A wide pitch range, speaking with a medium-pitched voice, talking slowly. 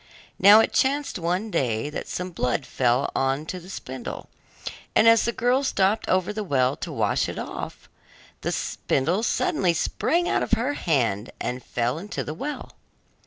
No: wide, 9.0 semitones; medium, 180 Hz; average, 170 wpm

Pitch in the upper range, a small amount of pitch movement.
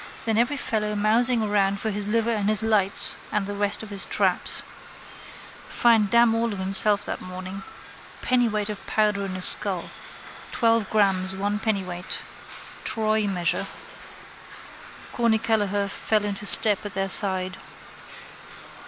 Yes: high, 210 Hz; narrow, 2.0 semitones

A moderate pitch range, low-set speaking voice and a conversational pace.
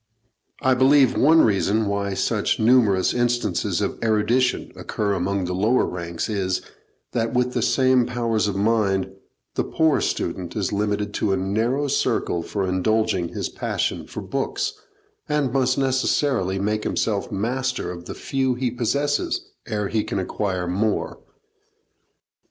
Yes: average, 4.6 semitones; low, 110 Hz; average, 145 wpm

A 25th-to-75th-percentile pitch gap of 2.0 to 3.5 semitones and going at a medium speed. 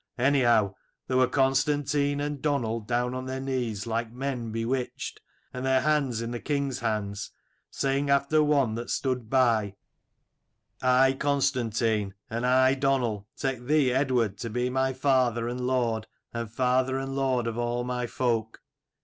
Yes: narrow, 2.5 semitones; average, 150 wpm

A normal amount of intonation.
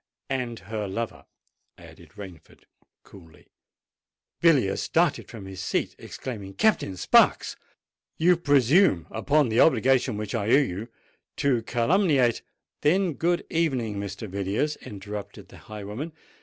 No: wide, 6.5 semitones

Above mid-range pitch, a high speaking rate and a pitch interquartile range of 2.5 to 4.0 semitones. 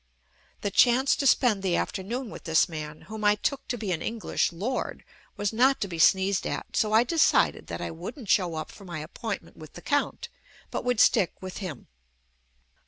No: high, 205 Hz; fast, 215 wpm; wide, 5.5 semitones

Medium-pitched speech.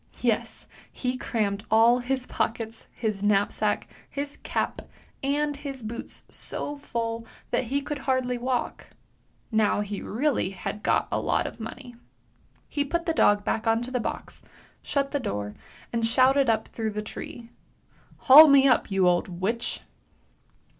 No: high, 240 Hz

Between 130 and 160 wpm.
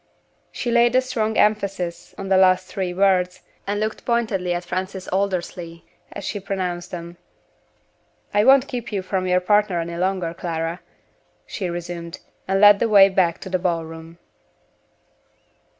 Yes: average, 155 wpm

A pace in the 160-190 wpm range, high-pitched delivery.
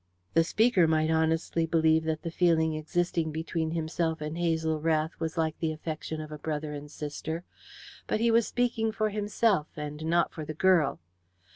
No: average, 170 wpm; medium, 160 Hz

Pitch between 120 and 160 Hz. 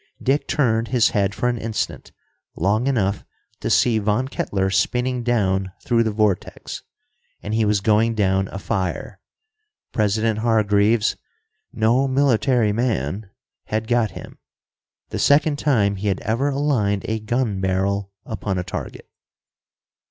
No: low, 110 Hz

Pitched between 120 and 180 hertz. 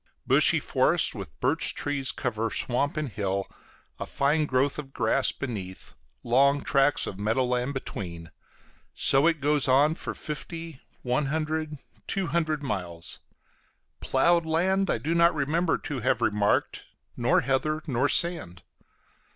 Yes: medium, 140 Hz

